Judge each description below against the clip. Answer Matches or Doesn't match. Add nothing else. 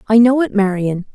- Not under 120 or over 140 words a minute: Doesn't match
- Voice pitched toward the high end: Matches